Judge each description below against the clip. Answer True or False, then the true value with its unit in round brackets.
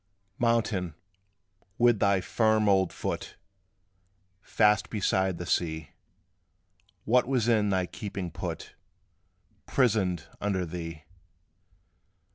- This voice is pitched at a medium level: False (100 Hz)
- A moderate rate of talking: False (90 wpm)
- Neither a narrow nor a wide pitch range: True (3.5 semitones)